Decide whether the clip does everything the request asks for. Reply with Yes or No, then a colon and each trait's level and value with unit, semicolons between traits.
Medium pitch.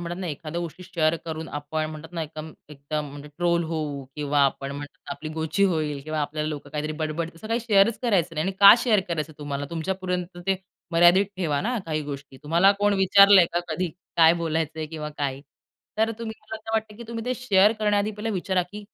Yes: medium, 165 Hz